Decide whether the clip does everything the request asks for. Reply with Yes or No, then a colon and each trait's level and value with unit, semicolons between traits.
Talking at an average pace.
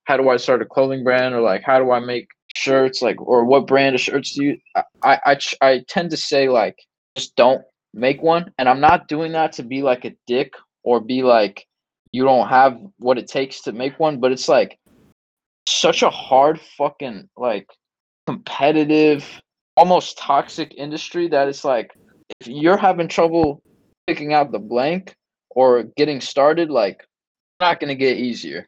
Yes: average, 180 wpm